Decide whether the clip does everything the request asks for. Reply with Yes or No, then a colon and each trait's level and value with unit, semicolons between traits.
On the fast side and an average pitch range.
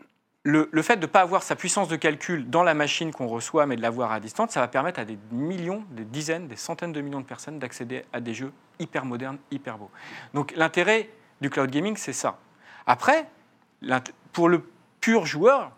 No: average, 210 wpm; average, 4.9 semitones